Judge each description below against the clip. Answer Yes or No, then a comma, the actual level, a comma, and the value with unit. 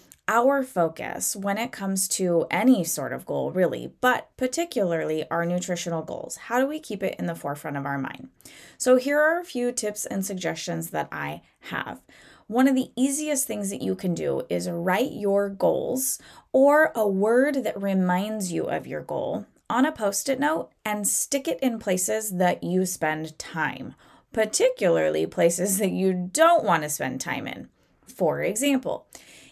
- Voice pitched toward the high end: Yes, high, 205 Hz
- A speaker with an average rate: Yes, average, 175 wpm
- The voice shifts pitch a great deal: Yes, wide, 6.6 semitones